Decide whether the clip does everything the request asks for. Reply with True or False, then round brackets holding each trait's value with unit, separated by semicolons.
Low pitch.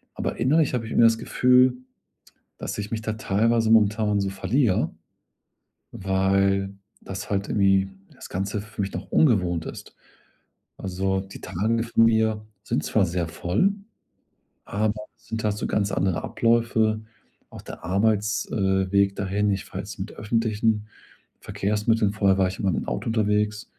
True (105 Hz)